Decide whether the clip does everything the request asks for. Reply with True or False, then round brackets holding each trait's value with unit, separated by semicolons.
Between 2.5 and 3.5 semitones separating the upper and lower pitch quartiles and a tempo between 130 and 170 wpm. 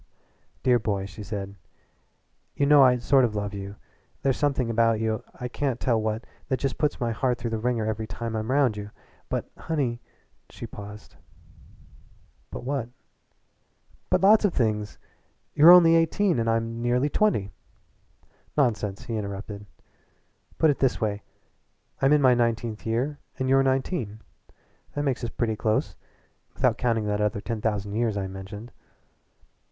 False (4.0 semitones; 165 wpm)